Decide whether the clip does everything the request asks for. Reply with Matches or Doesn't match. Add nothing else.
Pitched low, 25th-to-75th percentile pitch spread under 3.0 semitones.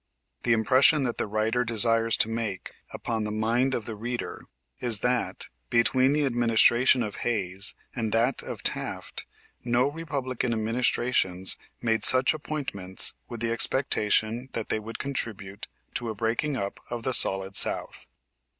Matches